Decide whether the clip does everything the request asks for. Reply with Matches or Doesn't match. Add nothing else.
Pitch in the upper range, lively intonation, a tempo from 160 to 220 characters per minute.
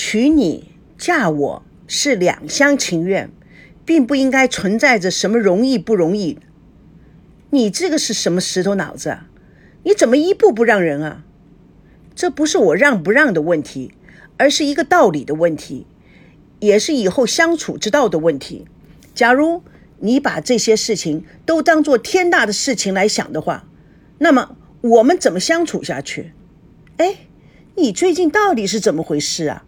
Doesn't match